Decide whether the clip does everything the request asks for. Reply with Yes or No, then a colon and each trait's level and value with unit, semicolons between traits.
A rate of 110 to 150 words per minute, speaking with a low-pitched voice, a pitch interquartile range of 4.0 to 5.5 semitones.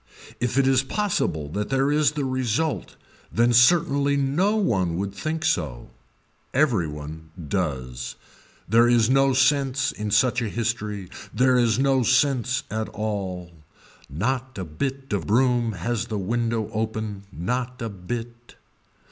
Yes: average, 140 wpm; low, 120 Hz; average, 4.9 semitones